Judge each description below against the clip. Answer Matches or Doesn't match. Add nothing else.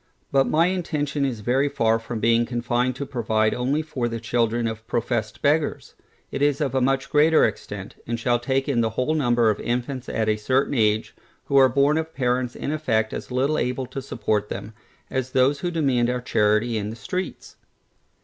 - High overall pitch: Doesn't match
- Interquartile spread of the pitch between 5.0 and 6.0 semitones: Doesn't match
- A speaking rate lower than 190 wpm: Doesn't match